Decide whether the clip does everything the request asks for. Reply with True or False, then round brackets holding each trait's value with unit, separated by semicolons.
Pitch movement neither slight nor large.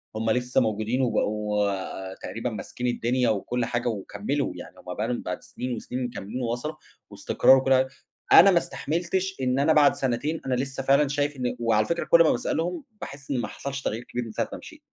True (3.6 semitones)